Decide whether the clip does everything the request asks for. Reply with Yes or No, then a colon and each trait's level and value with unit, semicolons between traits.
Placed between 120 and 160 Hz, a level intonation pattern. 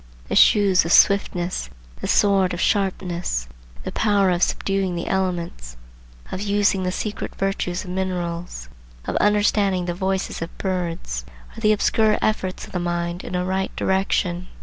No: medium, 185 Hz; narrow, 2.2 semitones